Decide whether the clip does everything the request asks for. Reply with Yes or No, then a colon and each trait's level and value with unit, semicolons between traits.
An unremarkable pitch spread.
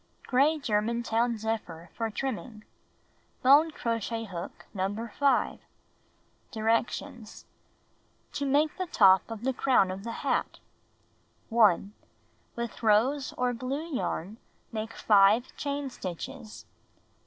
Yes: average, 3.8 semitones